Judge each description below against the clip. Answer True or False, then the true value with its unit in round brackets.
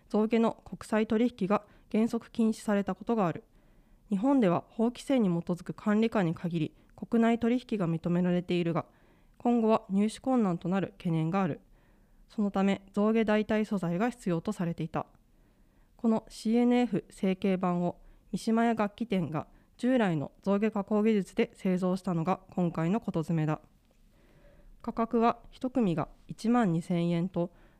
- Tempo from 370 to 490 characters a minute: False (285 characters per minute)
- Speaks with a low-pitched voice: False (200 Hz)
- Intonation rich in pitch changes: False (4.6 semitones)